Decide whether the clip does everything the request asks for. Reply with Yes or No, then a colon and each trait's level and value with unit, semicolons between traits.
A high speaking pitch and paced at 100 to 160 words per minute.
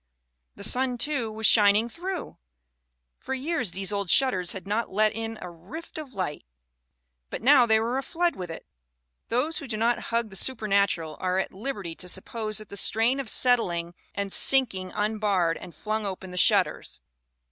No: high, 215 Hz; average, 175 wpm